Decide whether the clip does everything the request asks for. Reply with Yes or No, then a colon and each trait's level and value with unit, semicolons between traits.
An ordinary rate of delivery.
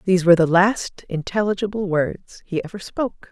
Yes: average, 165 wpm